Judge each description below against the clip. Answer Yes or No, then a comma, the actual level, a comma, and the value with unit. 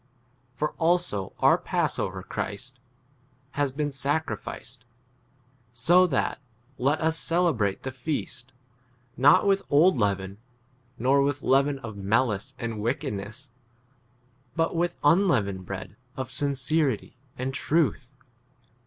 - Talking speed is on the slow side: Yes, slow, 115 wpm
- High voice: No, low, 135 Hz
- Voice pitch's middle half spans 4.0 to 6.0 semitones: Yes, average, 5.2 semitones